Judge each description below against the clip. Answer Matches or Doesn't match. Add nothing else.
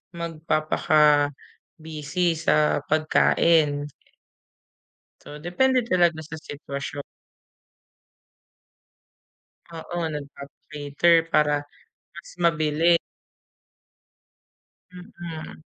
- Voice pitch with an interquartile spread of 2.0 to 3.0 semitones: Matches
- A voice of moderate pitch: Matches